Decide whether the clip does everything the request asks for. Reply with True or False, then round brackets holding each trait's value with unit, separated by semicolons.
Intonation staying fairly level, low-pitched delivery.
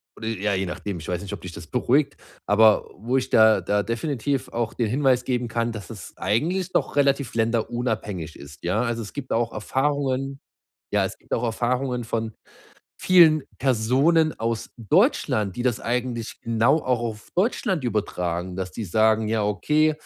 False (3.9 semitones; 115 Hz)